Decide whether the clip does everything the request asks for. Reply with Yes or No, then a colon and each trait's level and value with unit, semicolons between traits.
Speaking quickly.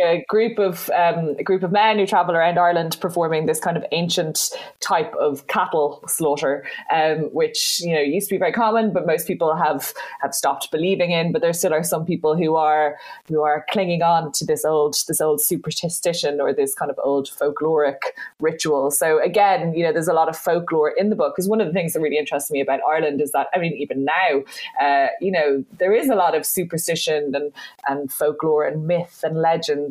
Yes: fast, 215 wpm